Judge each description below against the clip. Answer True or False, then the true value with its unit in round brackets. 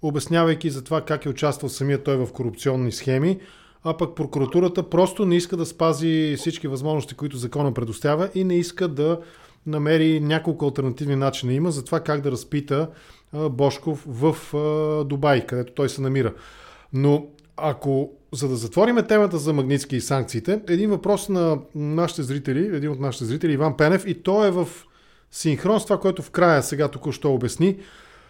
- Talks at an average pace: True (170 wpm)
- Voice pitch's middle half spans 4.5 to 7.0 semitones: False (3.4 semitones)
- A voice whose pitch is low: False (150 Hz)